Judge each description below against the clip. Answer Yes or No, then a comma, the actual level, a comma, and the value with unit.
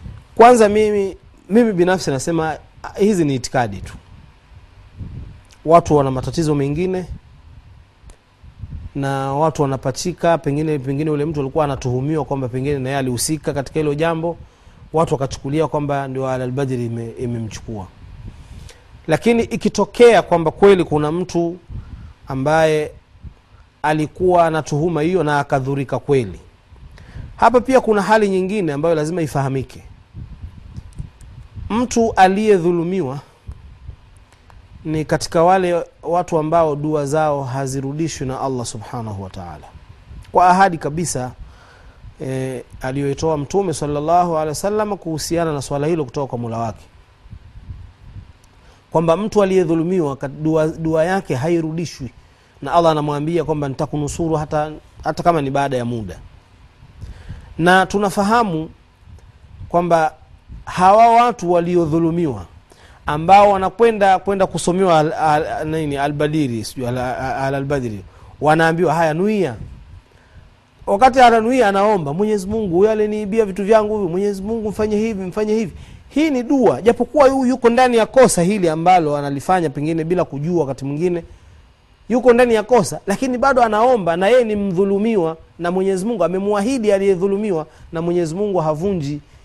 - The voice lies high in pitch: No, medium, 155 Hz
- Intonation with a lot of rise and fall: Yes, wide, 7.2 semitones